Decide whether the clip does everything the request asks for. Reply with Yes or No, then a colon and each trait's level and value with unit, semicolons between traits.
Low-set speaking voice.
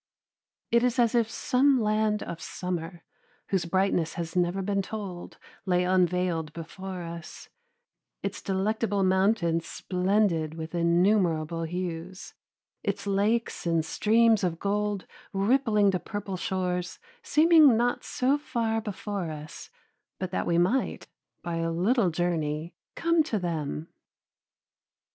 No: medium, 185 Hz